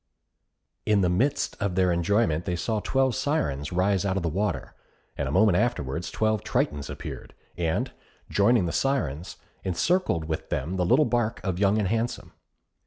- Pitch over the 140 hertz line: No, very low, 95 Hz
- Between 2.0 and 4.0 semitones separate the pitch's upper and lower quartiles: No, average, 4.9 semitones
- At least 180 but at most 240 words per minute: No, average, 170 wpm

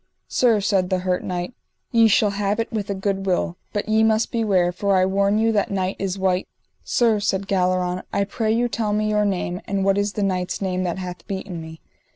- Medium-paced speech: No, fast, 220 wpm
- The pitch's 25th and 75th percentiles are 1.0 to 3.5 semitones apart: Yes, narrow, 2.4 semitones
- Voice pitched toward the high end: Yes, high, 195 Hz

